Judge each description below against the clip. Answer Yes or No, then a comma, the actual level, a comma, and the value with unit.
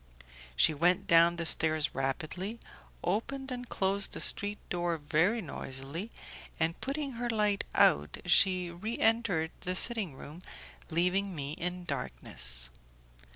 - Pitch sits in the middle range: Yes, medium, 180 Hz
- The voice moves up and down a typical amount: Yes, average, 4.8 semitones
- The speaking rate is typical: No, slow, 125 wpm